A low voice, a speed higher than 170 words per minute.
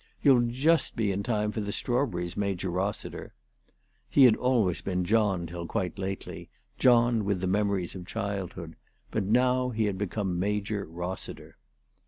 No: low, 100 Hz; average, 155 wpm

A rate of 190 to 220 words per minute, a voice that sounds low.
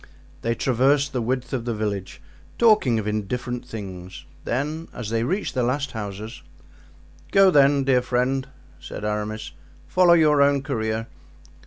No: average, 145 wpm; low, 125 Hz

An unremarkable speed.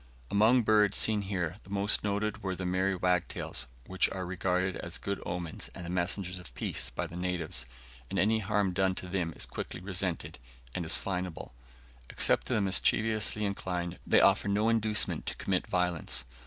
Yes: average, 175 wpm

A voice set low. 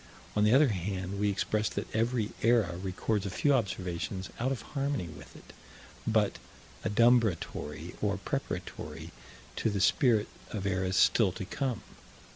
Yes: low, 105 Hz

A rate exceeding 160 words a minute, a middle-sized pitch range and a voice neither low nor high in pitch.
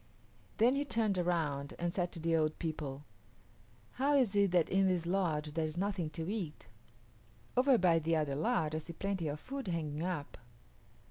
Yes: average, 185 wpm; average, 4.2 semitones; medium, 170 Hz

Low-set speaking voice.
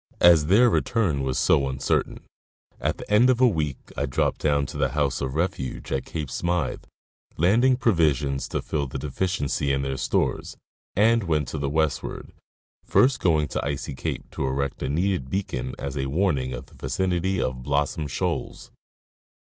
Yes: very low, 75 Hz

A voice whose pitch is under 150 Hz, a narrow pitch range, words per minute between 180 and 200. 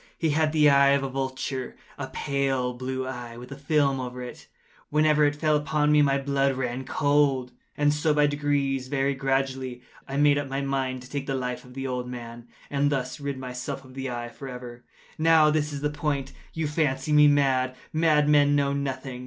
Yes: low, 135 Hz; narrow, 2.1 semitones; average, 190 wpm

